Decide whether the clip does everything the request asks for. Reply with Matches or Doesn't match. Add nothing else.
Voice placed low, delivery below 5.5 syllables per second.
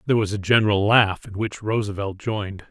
Doesn't match